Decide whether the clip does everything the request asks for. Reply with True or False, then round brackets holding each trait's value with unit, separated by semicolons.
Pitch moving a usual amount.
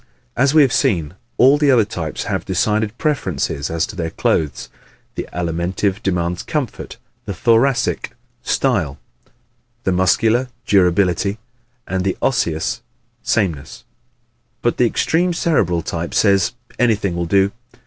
False (5.8 semitones)